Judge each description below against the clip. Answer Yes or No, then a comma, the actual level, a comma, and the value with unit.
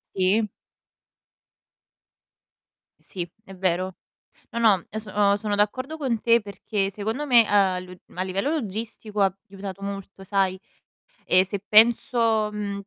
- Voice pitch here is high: Yes, high, 205 Hz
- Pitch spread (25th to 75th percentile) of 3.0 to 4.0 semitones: No, narrow, 2.5 semitones